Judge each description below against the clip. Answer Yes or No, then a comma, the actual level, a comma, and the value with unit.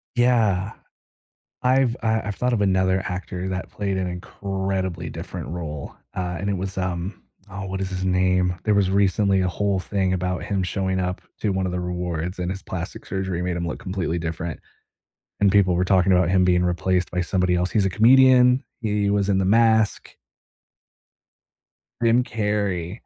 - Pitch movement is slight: Yes, narrow, 2.1 semitones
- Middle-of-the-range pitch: No, very low, 95 Hz